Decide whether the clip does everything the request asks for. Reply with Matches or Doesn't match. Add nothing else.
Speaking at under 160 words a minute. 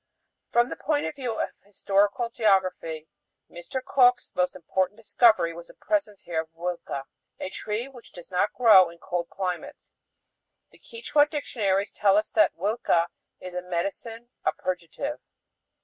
Matches